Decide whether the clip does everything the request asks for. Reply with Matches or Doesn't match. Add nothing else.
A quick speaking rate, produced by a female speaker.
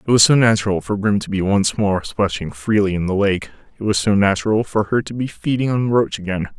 Doesn't match